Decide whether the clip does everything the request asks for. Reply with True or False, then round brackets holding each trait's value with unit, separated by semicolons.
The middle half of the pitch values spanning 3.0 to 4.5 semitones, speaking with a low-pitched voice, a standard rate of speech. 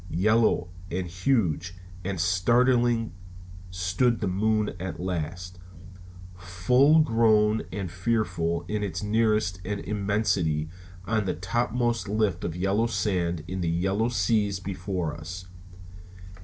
False (3.6 semitones; 95 Hz; 115 wpm)